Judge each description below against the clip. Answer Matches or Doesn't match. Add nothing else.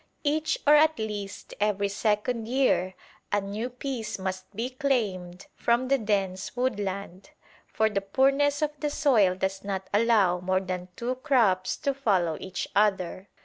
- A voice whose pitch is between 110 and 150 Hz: Doesn't match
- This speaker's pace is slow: Doesn't match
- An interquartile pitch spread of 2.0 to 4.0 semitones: Doesn't match